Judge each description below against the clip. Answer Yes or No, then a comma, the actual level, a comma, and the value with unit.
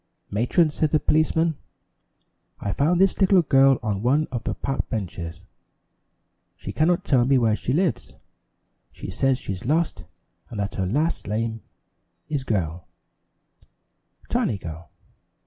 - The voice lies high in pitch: No, low, 130 Hz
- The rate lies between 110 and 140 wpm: Yes, slow, 135 wpm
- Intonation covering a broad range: Yes, wide, 7.3 semitones